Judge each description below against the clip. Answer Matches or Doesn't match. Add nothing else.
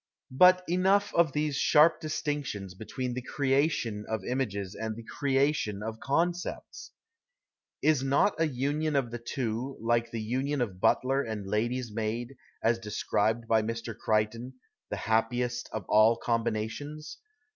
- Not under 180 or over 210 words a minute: Doesn't match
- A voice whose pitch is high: Doesn't match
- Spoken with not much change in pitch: Doesn't match